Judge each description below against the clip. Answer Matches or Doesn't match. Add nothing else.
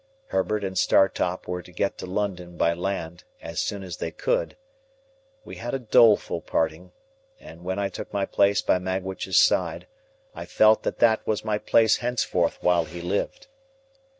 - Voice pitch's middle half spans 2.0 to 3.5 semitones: Matches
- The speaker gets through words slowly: Doesn't match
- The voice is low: Matches